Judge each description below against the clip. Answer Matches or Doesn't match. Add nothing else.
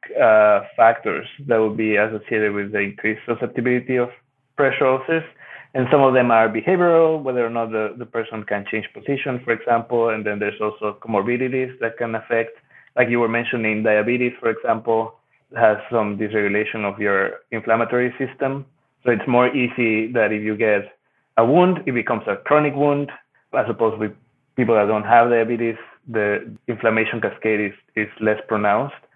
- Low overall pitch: Matches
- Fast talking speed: Doesn't match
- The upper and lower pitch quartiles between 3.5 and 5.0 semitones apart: Doesn't match